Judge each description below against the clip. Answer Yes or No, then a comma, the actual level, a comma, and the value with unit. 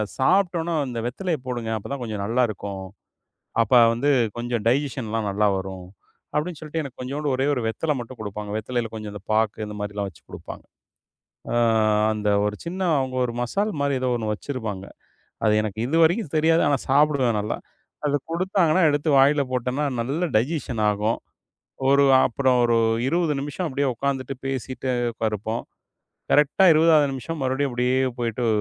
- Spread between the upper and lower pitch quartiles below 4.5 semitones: No, average, 5.0 semitones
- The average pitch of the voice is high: No, low, 130 Hz